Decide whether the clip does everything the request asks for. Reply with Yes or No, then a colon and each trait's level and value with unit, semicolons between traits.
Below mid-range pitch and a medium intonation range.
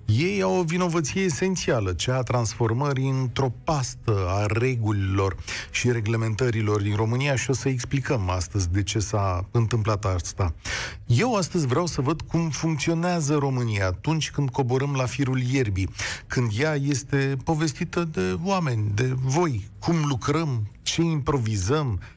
No: low, 130 Hz; wide, 5.9 semitones